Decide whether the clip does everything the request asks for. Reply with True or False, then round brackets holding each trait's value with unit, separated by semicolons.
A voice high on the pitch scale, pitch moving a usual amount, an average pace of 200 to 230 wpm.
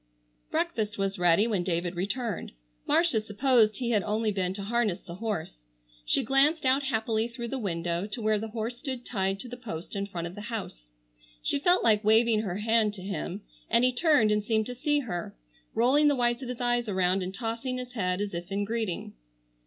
True (220 Hz; 3.7 semitones; 205 wpm)